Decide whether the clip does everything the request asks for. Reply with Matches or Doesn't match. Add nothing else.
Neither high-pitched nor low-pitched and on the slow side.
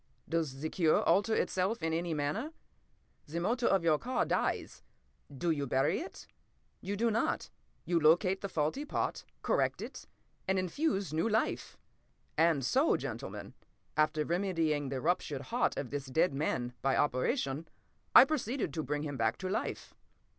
Doesn't match